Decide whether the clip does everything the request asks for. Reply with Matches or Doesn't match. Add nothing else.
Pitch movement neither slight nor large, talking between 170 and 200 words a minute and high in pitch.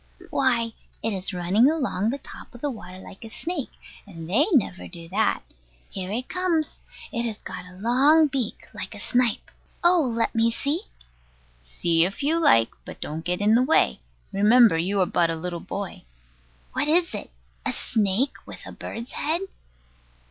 Doesn't match